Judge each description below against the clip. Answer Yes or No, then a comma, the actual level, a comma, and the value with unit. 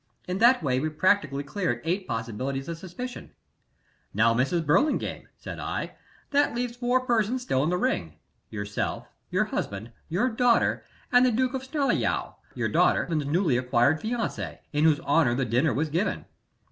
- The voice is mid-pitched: Yes, medium, 165 Hz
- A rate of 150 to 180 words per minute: Yes, average, 160 wpm